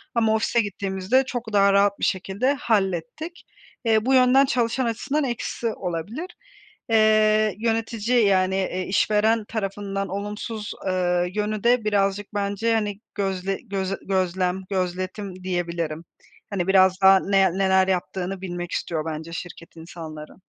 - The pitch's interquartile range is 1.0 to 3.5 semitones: Yes, average, 2.9 semitones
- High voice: Yes, high, 200 Hz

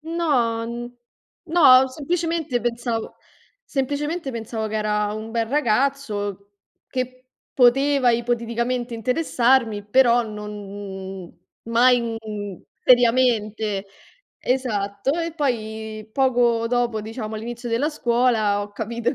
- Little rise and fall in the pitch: No, average, 3.0 semitones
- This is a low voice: No, high, 235 Hz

